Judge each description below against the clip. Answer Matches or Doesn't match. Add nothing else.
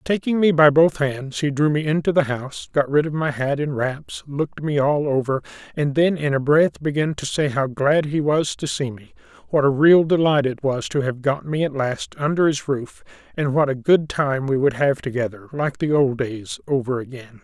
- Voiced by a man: Matches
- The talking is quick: Matches